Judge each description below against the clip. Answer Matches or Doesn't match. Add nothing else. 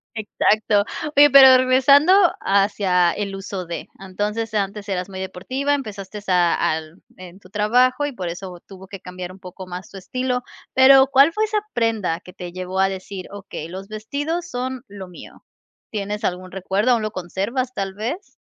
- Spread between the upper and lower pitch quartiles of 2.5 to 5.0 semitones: Doesn't match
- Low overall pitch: Doesn't match